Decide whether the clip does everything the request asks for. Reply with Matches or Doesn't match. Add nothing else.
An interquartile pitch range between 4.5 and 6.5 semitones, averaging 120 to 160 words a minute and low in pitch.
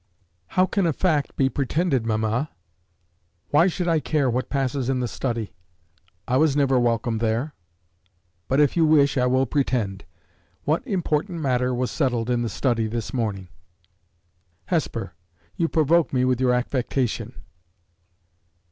Doesn't match